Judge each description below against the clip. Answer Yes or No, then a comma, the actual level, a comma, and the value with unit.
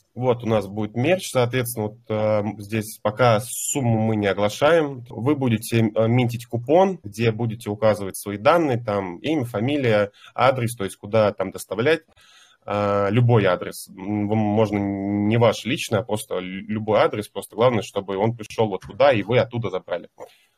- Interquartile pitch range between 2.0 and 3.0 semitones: Yes, average, 2.7 semitones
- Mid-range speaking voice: No, low, 110 Hz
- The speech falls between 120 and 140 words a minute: No, average, 155 wpm